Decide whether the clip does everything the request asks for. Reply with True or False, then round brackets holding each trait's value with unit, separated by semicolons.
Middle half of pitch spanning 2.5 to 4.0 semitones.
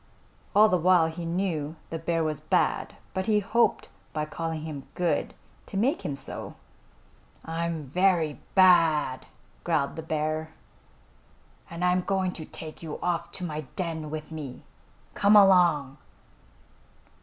True (2.8 semitones)